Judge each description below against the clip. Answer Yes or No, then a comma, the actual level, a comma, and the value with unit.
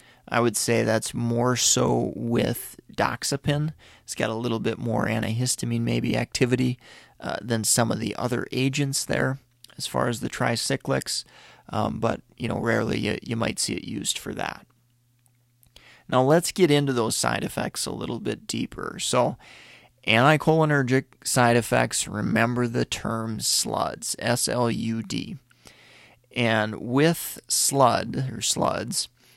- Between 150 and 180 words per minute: No, average, 140 wpm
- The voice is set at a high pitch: No, low, 120 Hz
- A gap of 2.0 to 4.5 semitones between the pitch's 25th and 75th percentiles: Yes, narrow, 2.6 semitones